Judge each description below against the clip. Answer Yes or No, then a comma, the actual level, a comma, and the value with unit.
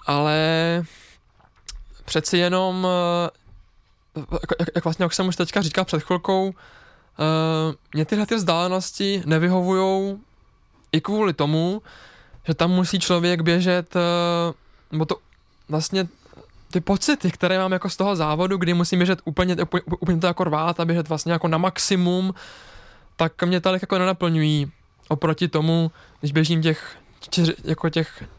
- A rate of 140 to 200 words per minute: No, average, 130 wpm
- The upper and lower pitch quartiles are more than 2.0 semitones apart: Yes, narrow, 2.6 semitones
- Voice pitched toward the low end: No, medium, 175 Hz